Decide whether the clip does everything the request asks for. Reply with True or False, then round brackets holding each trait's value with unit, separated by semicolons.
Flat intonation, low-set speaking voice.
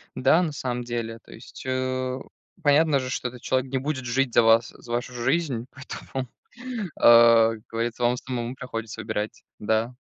True (2.1 semitones; 125 Hz)